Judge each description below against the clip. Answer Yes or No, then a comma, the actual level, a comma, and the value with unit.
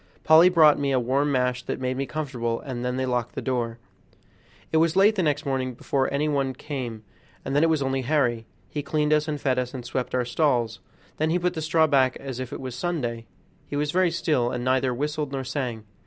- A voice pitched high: No, low, 135 Hz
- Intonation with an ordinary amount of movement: Yes, average, 3.3 semitones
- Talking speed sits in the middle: No, fast, 240 wpm